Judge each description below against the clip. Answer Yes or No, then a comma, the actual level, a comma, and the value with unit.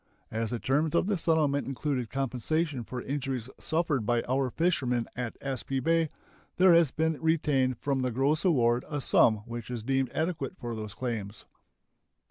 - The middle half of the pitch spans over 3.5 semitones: Yes, average, 4.5 semitones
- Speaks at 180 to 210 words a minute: No, average, 165 wpm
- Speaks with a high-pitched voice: No, low, 135 Hz